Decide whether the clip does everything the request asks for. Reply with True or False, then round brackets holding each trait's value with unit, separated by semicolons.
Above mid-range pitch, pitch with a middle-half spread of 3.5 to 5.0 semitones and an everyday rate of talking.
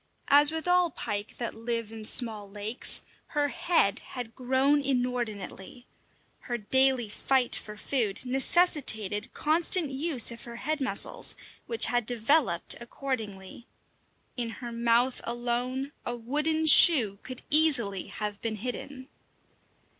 False (245 Hz; 3.9 semitones; 125 wpm)